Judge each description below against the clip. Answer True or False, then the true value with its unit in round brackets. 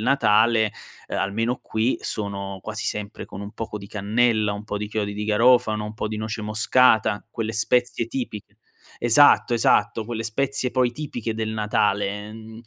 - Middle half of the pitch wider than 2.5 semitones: False (2.0 semitones)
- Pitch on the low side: True (110 Hz)